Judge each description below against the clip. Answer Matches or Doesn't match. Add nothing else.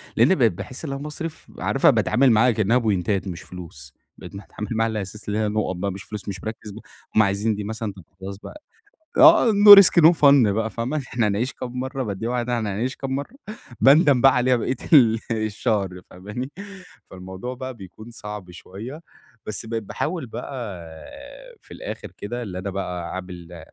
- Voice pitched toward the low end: Matches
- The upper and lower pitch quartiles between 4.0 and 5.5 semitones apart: Matches